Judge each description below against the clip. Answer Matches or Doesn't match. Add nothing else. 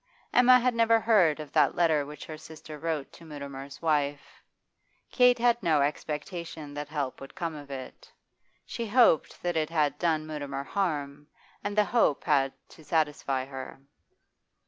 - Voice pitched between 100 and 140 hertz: Doesn't match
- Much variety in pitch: Doesn't match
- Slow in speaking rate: Doesn't match